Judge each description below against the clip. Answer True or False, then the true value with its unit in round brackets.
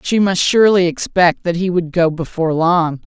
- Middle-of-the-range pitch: True (175 Hz)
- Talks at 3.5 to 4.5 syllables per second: False (5.1 syllables/s)